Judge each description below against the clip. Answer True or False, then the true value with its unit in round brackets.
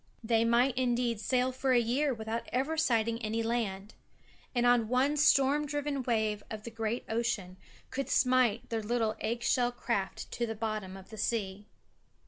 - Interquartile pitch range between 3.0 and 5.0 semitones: False (2.5 semitones)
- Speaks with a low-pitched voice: False (235 Hz)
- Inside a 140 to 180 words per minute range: True (165 wpm)